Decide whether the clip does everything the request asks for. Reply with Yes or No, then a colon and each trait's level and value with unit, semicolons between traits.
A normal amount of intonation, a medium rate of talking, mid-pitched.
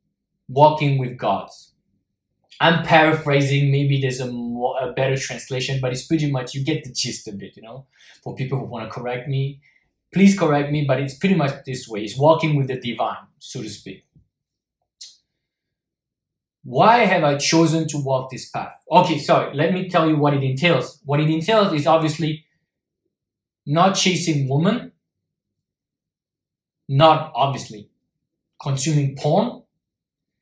Yes: average, 3.4 semitones; average, 150 wpm; medium, 145 Hz